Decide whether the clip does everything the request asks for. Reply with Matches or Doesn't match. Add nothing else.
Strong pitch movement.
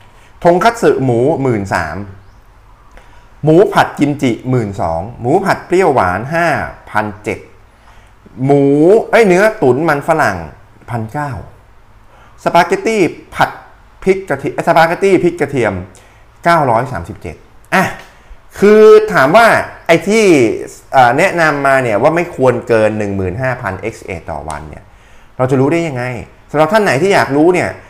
Matches